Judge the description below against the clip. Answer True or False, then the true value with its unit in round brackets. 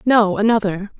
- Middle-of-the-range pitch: False (210 Hz)